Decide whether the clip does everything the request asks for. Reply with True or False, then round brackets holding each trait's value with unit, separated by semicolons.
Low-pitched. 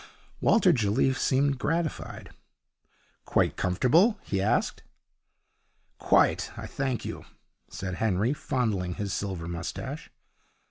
True (115 Hz)